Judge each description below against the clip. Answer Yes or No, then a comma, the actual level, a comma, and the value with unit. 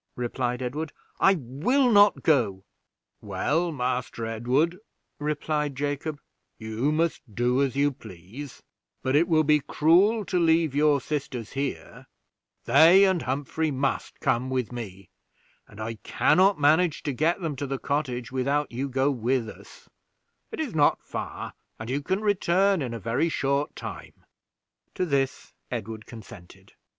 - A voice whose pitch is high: No, medium, 140 Hz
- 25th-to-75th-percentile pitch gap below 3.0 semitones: No, average, 4.5 semitones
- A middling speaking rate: Yes, average, 150 wpm